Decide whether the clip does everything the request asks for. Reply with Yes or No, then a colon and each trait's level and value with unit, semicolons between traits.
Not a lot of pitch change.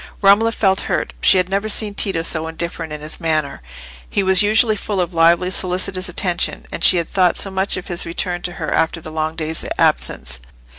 No: average, 3.0 semitones